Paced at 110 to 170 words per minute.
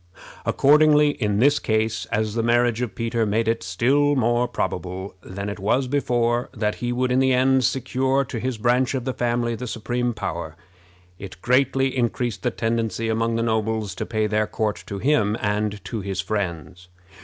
No: average, 180 wpm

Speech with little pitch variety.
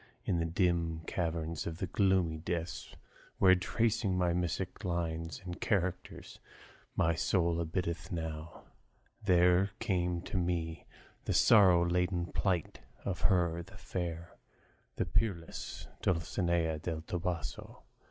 Yes: narrow, 1.8 semitones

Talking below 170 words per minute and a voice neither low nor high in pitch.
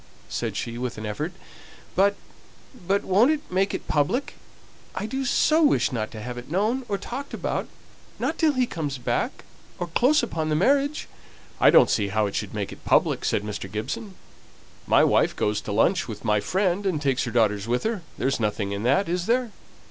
No: average, 200 wpm; medium, 165 Hz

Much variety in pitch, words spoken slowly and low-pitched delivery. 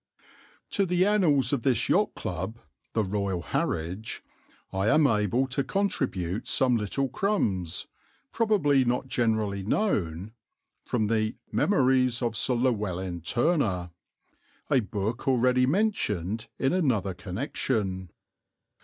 Yes: wide, 5.7 semitones; slow, 115 wpm; low, 115 Hz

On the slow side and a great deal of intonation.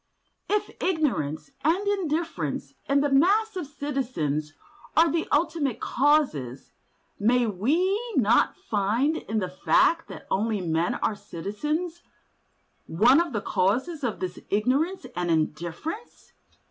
Yes: slow, 120 wpm; wide, 8.9 semitones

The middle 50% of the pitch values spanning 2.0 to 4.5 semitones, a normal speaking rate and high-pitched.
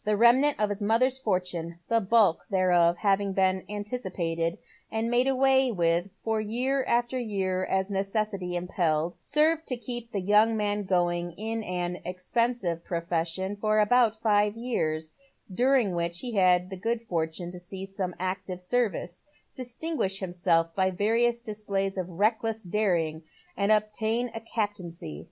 Yes: average, 4.1 semitones; average, 155 wpm; high, 200 Hz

